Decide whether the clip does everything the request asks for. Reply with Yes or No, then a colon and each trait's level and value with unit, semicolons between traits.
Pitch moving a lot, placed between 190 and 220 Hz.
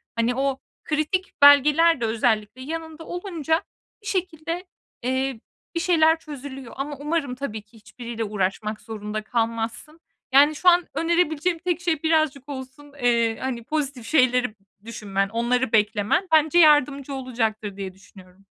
No: wide, 5.7 semitones; very high, 270 Hz